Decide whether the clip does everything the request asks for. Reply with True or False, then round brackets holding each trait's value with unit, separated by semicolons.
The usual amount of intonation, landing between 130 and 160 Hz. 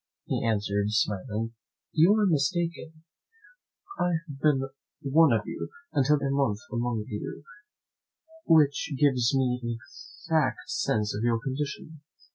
True (4.8 semitones; 135 Hz)